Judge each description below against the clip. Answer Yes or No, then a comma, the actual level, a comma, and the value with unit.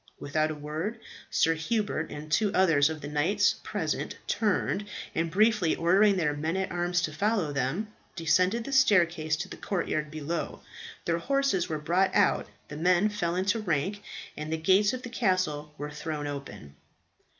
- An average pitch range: Yes, average, 4.8 semitones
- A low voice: No, medium, 170 Hz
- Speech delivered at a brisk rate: No, average, 170 wpm